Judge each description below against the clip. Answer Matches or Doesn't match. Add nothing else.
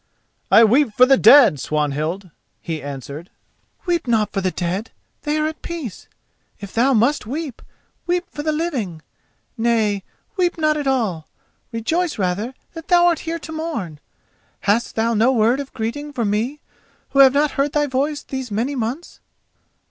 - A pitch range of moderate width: Doesn't match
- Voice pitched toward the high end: Matches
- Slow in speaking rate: Doesn't match